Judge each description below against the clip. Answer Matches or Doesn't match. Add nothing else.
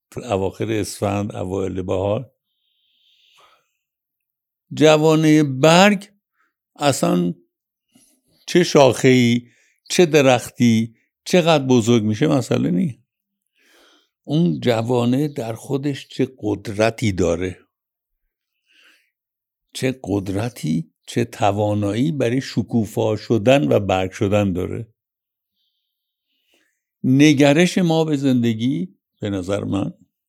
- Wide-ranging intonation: Matches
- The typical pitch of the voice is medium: Doesn't match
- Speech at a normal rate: Doesn't match